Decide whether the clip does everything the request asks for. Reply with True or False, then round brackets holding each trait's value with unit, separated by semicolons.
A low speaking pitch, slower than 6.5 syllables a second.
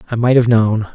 True (115 Hz; 5.9 syllables/s)